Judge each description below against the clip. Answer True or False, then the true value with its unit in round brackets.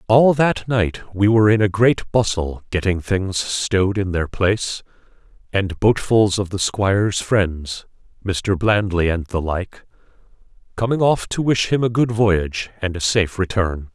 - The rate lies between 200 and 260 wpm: False (165 wpm)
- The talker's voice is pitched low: True (100 Hz)